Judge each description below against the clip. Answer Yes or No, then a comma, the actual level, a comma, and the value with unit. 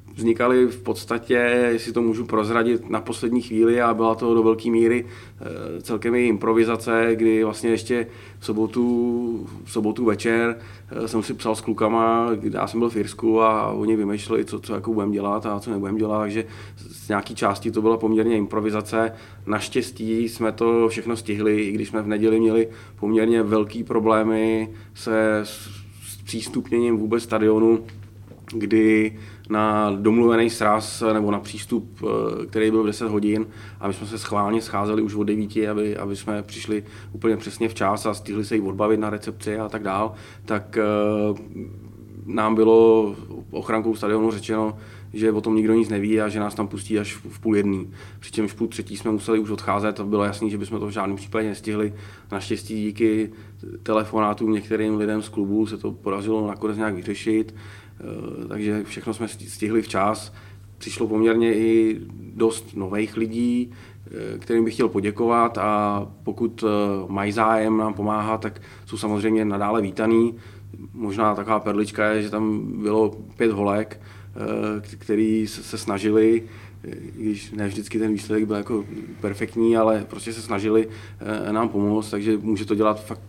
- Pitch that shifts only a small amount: Yes, narrow, 1.3 semitones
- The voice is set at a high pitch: No, low, 110 Hz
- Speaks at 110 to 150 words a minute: No, average, 160 wpm